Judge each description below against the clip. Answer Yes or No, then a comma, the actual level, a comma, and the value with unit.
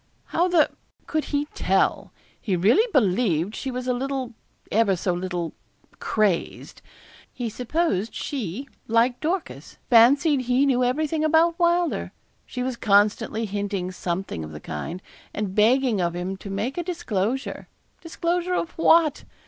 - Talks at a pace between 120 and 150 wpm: Yes, average, 140 wpm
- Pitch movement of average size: No, wide, 7.5 semitones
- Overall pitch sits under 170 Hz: No, high, 245 Hz